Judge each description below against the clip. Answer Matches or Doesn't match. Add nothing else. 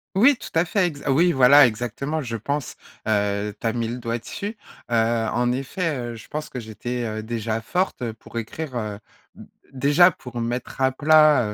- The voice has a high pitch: Doesn't match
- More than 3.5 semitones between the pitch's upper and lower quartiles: Matches